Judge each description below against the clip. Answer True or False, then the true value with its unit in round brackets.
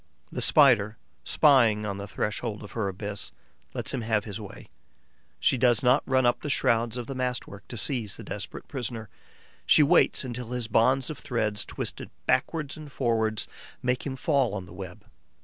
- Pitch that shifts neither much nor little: True (3.6 semitones)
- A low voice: True (115 Hz)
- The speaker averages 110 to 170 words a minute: False (185 wpm)